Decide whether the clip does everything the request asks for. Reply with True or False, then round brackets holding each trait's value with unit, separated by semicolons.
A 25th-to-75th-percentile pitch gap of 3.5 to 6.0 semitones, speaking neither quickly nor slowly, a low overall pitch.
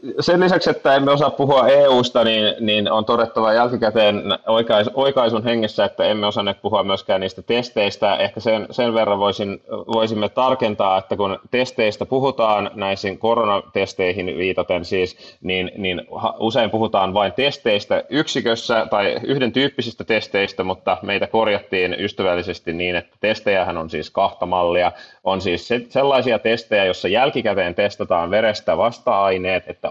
True (4.0 semitones; 140 wpm; 110 Hz)